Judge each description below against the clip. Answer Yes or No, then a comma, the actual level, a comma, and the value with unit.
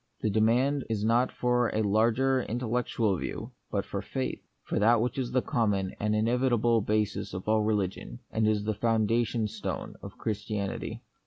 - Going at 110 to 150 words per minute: No, average, 165 wpm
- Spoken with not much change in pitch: Yes, narrow, 2.2 semitones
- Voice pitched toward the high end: No, low, 110 Hz